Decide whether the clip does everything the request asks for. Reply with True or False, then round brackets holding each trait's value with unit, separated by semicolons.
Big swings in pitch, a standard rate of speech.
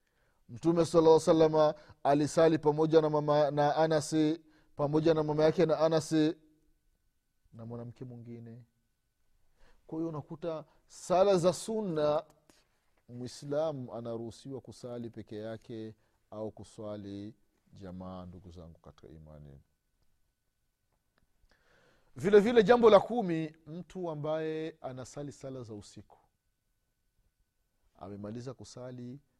False (5.9 semitones; 95 wpm)